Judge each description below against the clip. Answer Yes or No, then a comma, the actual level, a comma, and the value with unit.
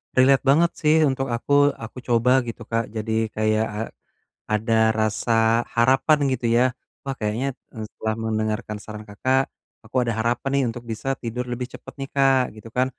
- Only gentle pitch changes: No, average, 3.3 semitones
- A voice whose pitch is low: Yes, low, 115 Hz